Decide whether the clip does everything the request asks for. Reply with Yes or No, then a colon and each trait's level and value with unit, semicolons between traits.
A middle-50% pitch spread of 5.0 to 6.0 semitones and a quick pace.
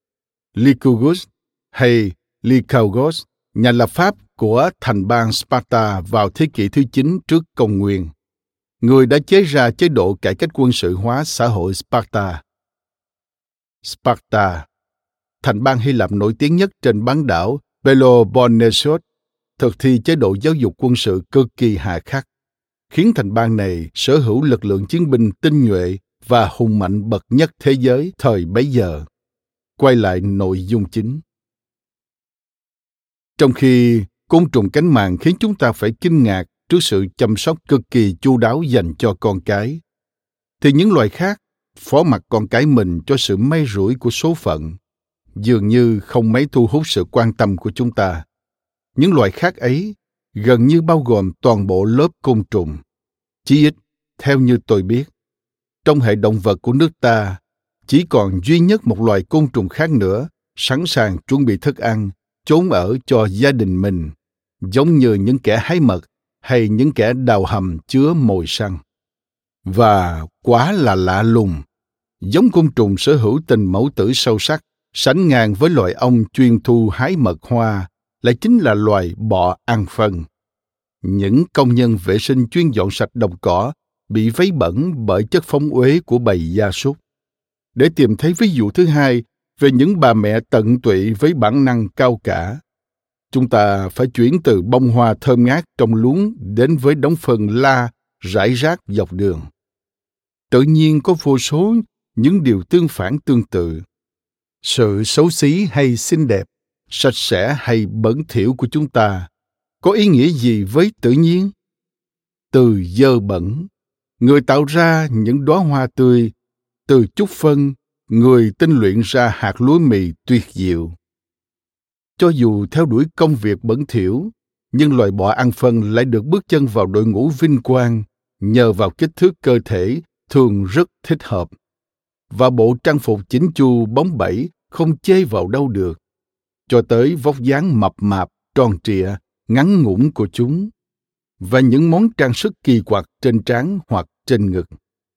No: wide, 5.5 semitones; average, 170 wpm